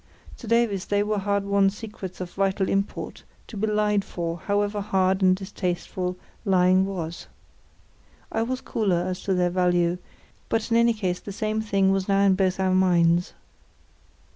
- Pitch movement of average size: No, narrow, 2.1 semitones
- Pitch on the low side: No, high, 195 Hz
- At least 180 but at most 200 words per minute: No, average, 165 wpm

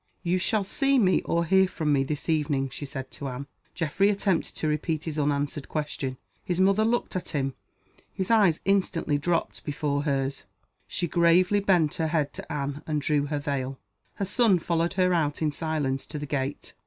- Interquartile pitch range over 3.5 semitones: Yes, average, 4.3 semitones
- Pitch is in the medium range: Yes, medium, 155 Hz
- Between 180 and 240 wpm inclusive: Yes, average, 190 wpm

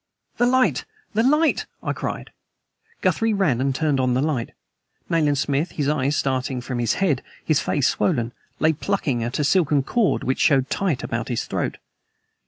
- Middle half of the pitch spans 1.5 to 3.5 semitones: No, average, 5.2 semitones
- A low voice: No, medium, 145 Hz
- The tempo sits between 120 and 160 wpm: No, average, 175 wpm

